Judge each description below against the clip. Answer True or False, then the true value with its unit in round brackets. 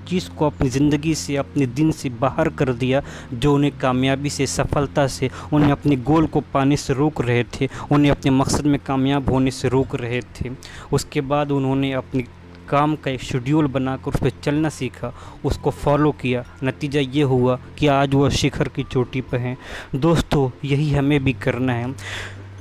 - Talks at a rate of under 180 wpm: False (185 wpm)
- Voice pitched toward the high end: False (135 Hz)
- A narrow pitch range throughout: True (2.1 semitones)